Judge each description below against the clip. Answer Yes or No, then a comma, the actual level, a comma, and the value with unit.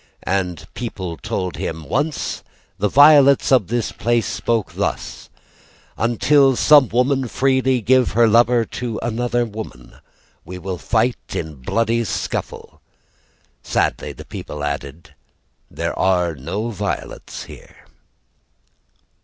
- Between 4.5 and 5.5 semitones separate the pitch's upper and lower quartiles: Yes, average, 5.1 semitones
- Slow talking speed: Yes, slow, 115 wpm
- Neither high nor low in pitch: No, low, 115 Hz